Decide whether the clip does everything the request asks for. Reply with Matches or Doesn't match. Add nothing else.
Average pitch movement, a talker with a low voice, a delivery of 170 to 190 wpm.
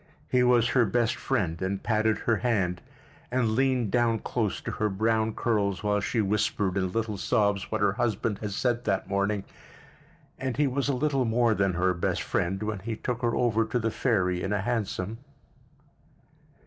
Matches